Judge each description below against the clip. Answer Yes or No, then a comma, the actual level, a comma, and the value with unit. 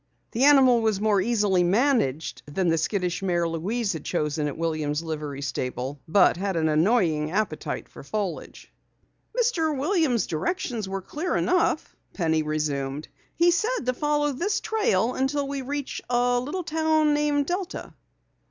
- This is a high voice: Yes, high, 215 Hz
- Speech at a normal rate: Yes, average, 150 wpm